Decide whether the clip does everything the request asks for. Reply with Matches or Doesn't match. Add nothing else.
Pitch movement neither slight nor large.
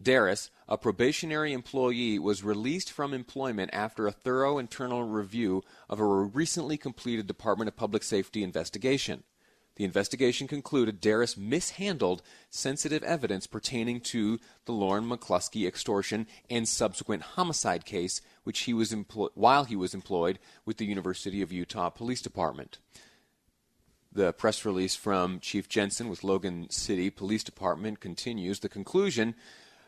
Matches